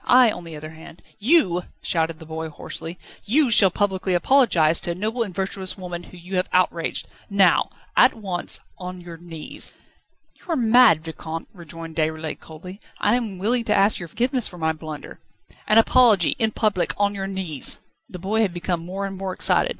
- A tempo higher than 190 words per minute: Yes, average, 200 wpm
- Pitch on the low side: No, medium, 185 Hz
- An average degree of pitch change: Yes, average, 4.2 semitones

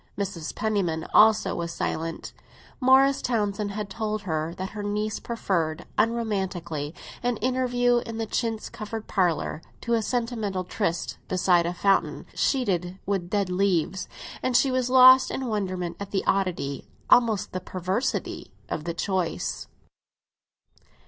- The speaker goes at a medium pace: No, slow, 130 wpm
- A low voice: No, high, 200 Hz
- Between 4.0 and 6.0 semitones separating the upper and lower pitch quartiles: Yes, average, 4.5 semitones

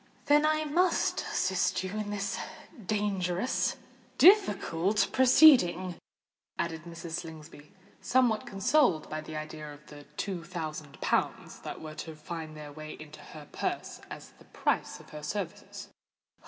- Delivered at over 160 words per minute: No, slow, 135 wpm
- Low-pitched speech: No, medium, 175 Hz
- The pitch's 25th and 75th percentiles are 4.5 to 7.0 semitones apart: Yes, average, 5.2 semitones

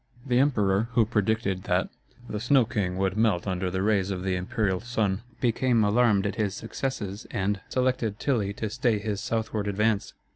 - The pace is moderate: Yes, average, 180 wpm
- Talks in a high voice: No, low, 105 Hz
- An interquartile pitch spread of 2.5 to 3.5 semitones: Yes, average, 3.0 semitones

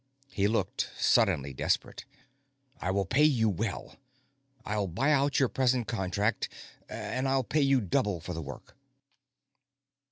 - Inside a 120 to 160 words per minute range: Yes, slow, 135 wpm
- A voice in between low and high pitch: No, low, 110 Hz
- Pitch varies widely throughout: Yes, wide, 5.7 semitones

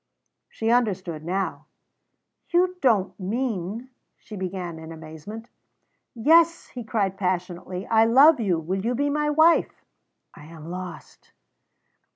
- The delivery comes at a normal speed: No, slow, 130 wpm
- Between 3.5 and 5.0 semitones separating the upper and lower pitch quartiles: No, wide, 5.6 semitones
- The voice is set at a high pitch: Yes, high, 200 Hz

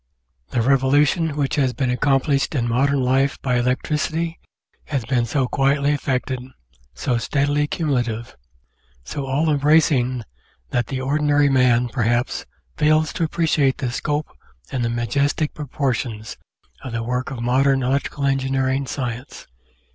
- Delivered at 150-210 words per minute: No, slow, 135 wpm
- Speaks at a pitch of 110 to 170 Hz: Yes, low, 135 Hz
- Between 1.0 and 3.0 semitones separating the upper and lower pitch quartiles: Yes, narrow, 2.5 semitones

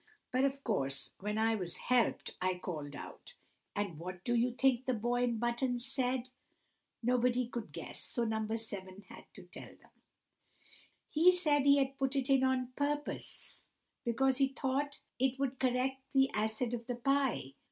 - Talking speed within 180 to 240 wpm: No, average, 170 wpm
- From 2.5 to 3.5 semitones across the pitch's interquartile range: Yes, average, 3.2 semitones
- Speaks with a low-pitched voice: No, very high, 250 Hz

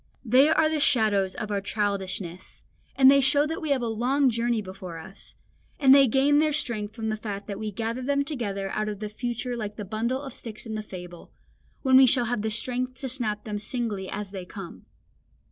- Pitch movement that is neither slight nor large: Yes, average, 4.2 semitones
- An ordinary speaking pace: No, fast, 215 wpm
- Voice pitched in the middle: No, high, 225 Hz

